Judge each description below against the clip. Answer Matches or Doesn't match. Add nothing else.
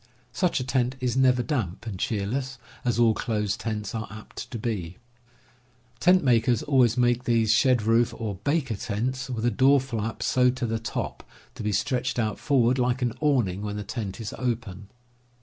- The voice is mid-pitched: Doesn't match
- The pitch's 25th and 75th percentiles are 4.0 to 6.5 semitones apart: Doesn't match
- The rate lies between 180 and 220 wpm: Matches